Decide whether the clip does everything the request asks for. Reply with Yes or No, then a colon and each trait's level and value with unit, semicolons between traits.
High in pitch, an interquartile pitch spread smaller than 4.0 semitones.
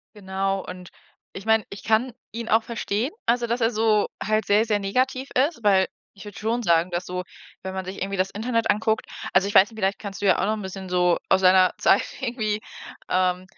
Yes: high, 205 Hz; average, 2.9 semitones